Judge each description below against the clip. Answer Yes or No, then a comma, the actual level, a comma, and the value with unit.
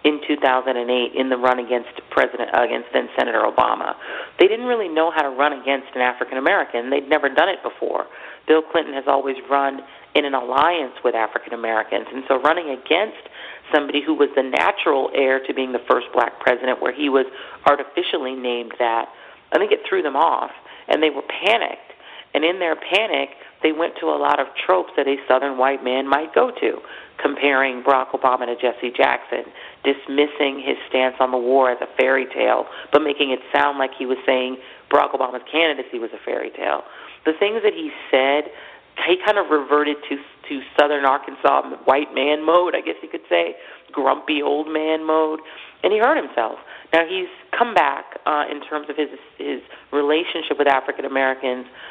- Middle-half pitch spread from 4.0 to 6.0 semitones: No, average, 3.1 semitones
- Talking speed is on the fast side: No, average, 190 wpm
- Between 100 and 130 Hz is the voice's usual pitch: No, medium, 140 Hz